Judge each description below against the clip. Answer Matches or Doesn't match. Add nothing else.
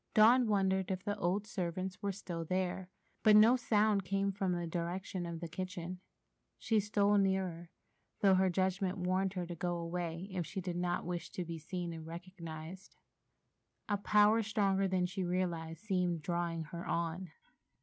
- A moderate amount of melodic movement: Doesn't match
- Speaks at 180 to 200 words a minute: Doesn't match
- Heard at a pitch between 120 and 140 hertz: Doesn't match